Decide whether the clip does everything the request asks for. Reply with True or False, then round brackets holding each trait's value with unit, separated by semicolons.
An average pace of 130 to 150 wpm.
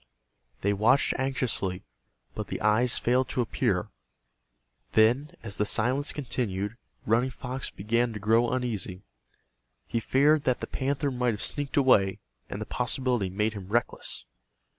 True (140 wpm)